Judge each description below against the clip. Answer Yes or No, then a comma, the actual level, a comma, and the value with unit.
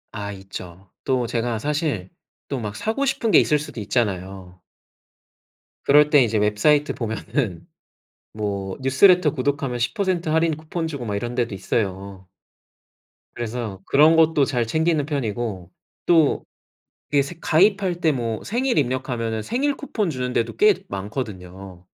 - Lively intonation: Yes, wide, 7.2 semitones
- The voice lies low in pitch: Yes, low, 125 Hz